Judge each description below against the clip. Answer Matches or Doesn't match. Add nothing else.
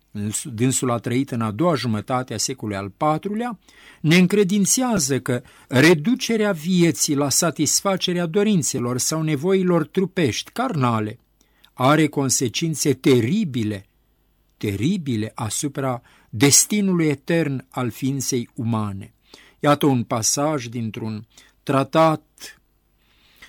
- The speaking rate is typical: Doesn't match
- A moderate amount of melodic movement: Doesn't match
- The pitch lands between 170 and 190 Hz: Doesn't match